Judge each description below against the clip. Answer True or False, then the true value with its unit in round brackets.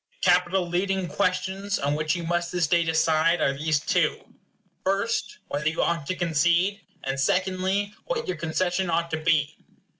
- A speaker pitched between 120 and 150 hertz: False (175 Hz)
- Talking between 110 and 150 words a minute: False (170 wpm)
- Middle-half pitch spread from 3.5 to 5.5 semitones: False (3.0 semitones)